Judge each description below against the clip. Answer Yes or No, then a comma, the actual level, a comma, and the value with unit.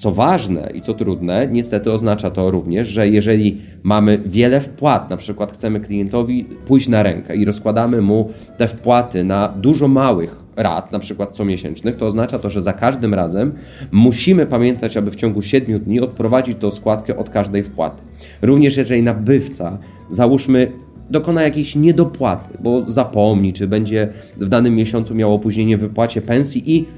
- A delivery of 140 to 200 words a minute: Yes, fast, 160 wpm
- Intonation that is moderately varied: Yes, average, 3.2 semitones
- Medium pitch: No, low, 110 Hz